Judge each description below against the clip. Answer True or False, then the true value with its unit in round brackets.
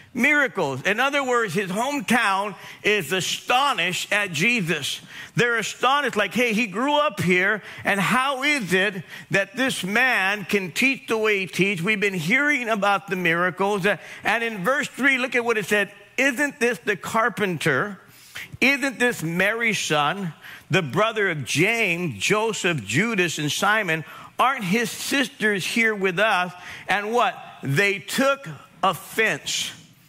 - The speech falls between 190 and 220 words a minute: False (150 wpm)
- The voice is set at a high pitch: True (205 Hz)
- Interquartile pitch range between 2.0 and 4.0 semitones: False (4.6 semitones)